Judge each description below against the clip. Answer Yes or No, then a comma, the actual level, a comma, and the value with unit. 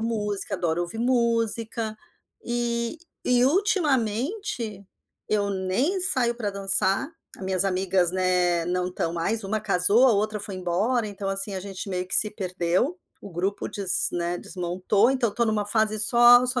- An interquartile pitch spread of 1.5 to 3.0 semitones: No, average, 4.1 semitones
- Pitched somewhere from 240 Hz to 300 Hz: No, high, 205 Hz